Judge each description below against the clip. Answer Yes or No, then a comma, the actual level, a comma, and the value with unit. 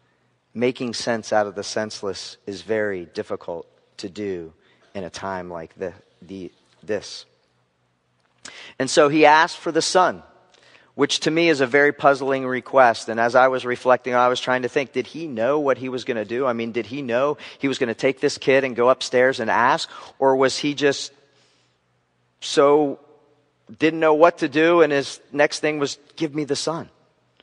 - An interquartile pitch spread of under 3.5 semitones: No, average, 4.5 semitones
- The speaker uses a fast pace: No, average, 195 wpm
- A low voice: Yes, low, 130 Hz